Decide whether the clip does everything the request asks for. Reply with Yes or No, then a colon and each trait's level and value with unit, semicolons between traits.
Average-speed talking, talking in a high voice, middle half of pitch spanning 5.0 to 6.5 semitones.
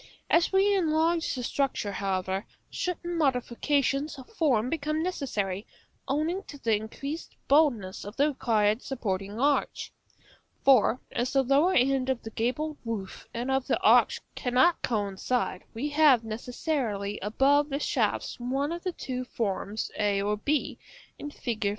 Yes: average, 145 wpm; very high, 260 Hz; wide, 5.4 semitones